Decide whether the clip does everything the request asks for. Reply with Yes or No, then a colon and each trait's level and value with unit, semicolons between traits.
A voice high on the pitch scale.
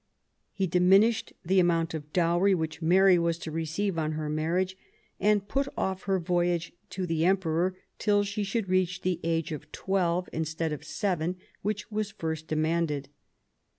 No: medium, 175 Hz